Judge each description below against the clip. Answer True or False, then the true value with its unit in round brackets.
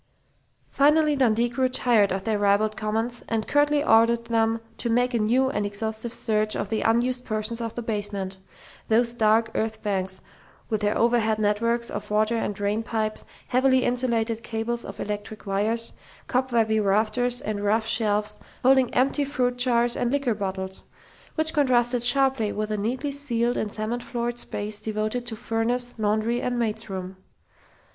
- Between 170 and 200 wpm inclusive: False (160 wpm)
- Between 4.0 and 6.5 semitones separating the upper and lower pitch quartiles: False (2.4 semitones)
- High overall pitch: True (225 Hz)